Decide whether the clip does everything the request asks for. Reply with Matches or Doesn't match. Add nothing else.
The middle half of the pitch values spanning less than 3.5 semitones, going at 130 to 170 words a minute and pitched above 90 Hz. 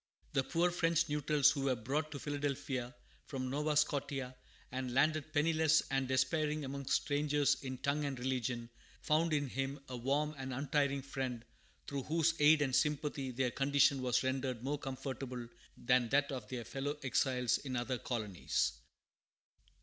Matches